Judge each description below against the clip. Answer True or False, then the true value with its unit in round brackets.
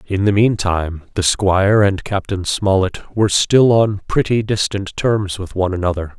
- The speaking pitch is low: True (100 Hz)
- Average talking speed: True (165 wpm)